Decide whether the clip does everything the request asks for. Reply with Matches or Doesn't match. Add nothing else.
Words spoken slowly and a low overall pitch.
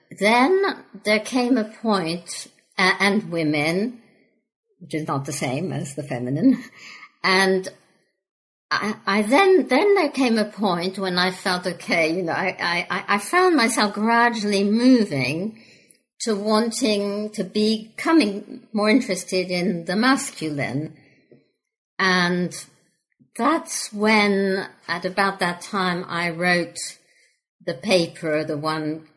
Doesn't match